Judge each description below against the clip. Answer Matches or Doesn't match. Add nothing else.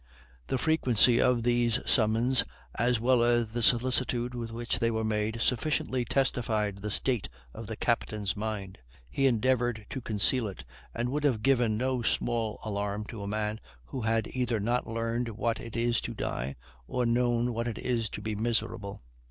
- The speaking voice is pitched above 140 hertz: Doesn't match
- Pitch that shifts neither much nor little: Doesn't match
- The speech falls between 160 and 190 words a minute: Matches